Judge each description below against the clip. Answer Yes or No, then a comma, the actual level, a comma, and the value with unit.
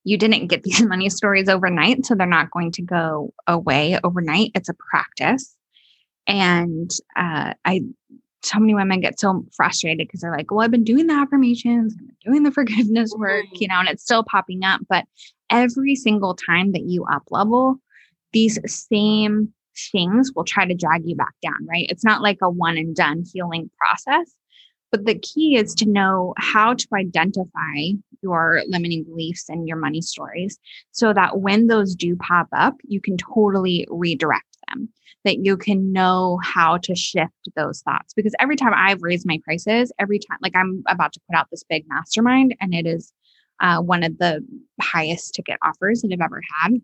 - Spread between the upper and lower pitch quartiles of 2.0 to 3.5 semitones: No, average, 4.5 semitones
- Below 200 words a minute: Yes, average, 185 wpm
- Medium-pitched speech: No, high, 195 Hz